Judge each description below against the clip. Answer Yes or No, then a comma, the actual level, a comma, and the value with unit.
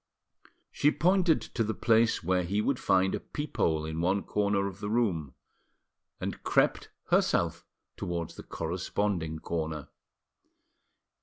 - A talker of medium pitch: No, very low, 95 Hz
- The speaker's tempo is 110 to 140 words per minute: Yes, slow, 135 wpm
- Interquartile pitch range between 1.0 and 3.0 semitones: No, average, 5.1 semitones